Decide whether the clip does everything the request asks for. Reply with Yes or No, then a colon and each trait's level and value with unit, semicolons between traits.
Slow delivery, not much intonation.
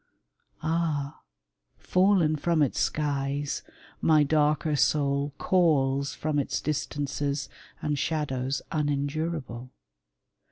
Yes: slow, 90 wpm; narrow, 1.9 semitones